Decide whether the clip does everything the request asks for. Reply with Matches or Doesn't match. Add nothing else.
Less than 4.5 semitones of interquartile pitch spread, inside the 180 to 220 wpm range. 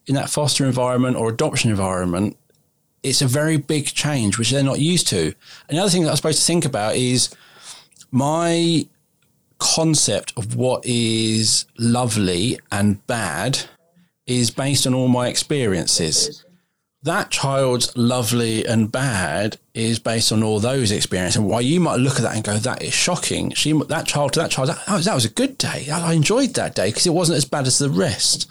Doesn't match